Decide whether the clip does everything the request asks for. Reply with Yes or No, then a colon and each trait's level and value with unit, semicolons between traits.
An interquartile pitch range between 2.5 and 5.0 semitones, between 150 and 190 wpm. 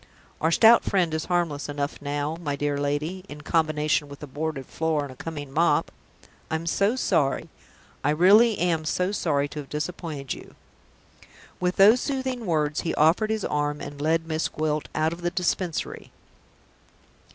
Yes: average, 3.3 semitones; average, 165 wpm